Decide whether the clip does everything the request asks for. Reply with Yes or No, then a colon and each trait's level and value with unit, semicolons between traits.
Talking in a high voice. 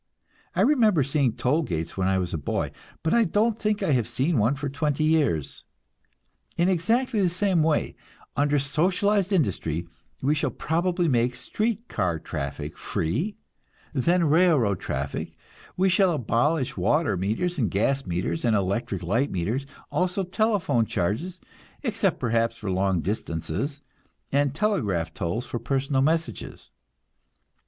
No: medium, 140 Hz